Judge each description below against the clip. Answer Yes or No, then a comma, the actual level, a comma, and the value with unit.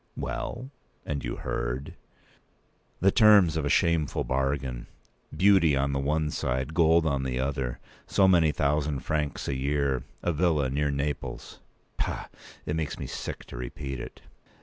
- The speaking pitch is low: Yes, very low, 70 Hz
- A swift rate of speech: No, average, 145 wpm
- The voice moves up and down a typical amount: Yes, average, 3.0 semitones